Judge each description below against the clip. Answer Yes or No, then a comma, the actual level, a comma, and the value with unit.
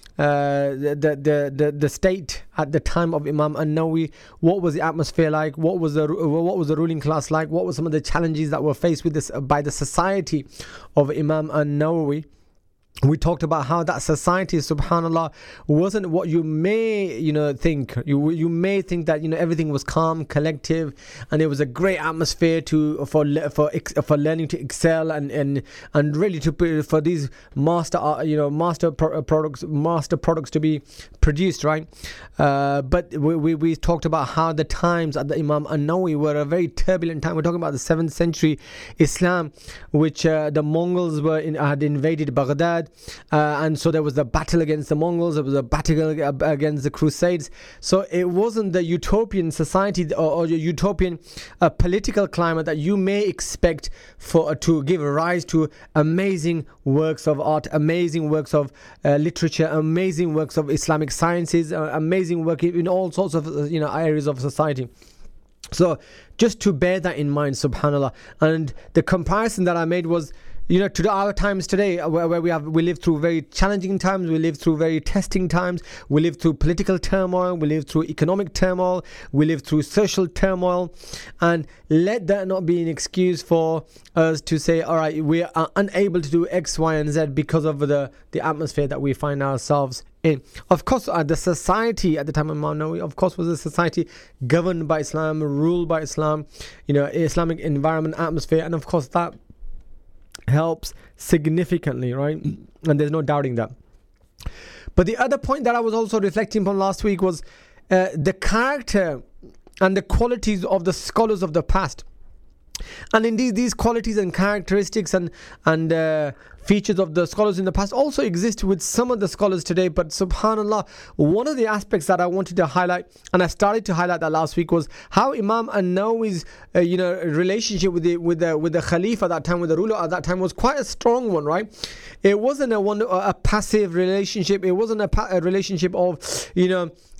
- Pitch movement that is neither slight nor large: Yes, average, 3.1 semitones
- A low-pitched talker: No, medium, 165 Hz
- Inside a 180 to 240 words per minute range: Yes, average, 190 wpm